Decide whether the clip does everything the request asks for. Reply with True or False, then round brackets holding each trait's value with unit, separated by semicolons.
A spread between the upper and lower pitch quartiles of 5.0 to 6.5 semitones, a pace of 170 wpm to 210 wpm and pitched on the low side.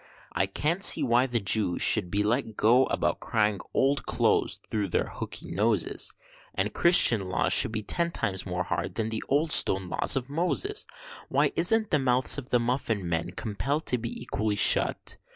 True (5.3 semitones; 185 wpm; 115 Hz)